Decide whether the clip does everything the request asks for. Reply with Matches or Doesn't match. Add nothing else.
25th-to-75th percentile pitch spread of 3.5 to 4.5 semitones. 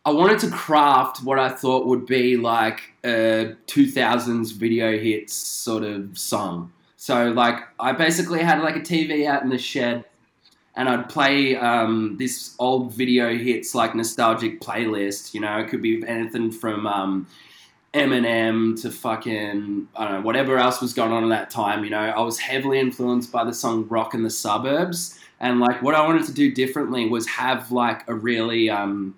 Doesn't match